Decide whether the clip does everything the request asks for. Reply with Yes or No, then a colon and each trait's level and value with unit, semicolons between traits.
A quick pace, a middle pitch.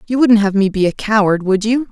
No: fast, 280 wpm; high, 210 Hz